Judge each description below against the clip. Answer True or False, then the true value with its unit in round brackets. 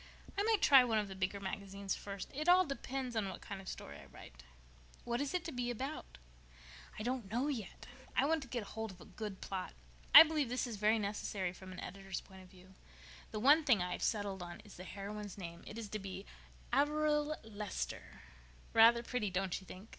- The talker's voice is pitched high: True (215 Hz)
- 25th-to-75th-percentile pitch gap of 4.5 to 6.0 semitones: True (5.2 semitones)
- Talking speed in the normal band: False (220 wpm)